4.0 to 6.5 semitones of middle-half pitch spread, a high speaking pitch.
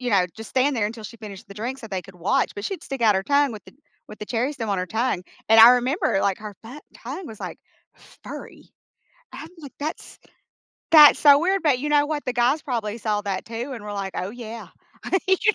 Yes: average, 5.3 semitones; high, 230 Hz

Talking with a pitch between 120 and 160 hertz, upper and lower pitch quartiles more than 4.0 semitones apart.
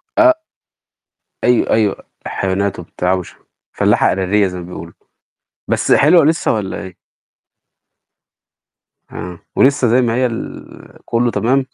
No: low, 110 Hz; wide, 5.4 semitones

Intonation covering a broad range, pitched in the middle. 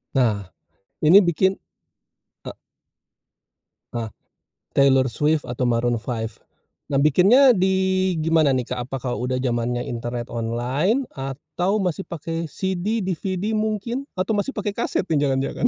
Yes: wide, 7.3 semitones; medium, 155 Hz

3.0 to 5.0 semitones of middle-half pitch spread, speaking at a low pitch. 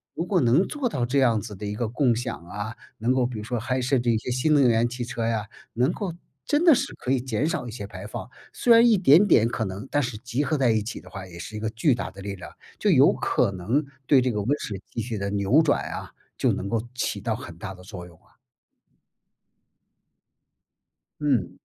Yes: average, 4.5 semitones; low, 120 Hz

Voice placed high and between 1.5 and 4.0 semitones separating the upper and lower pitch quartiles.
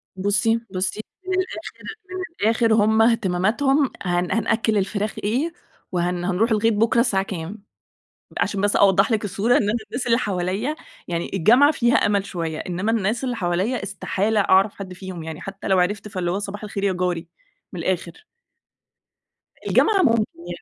Yes: high, 205 Hz; average, 3.6 semitones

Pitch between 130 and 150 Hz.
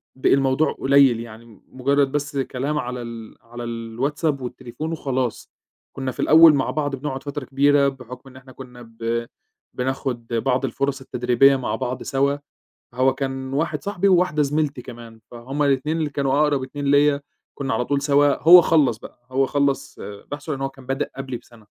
Yes: low, 135 Hz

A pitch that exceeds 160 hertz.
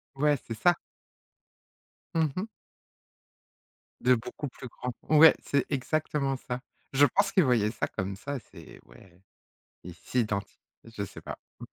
No: low, 130 Hz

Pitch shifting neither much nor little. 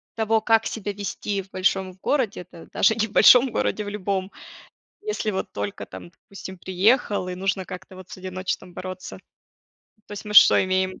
No: narrow, 2.3 semitones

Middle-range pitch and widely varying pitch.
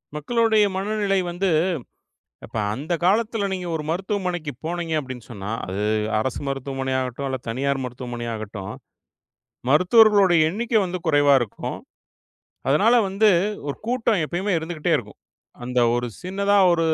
Yes: medium, 165 Hz; wide, 7.1 semitones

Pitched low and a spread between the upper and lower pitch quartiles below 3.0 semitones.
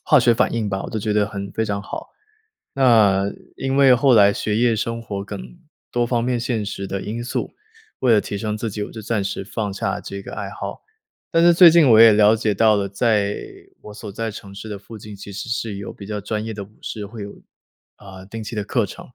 Yes: low, 105 Hz; narrow, 2.4 semitones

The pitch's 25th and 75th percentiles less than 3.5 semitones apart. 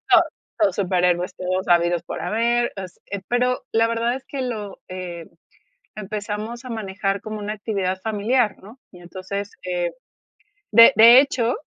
No: average, 4.0 semitones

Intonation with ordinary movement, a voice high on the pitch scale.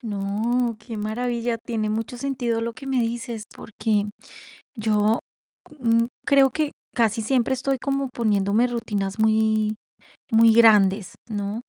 No: narrow, 2.2 semitones; high, 230 Hz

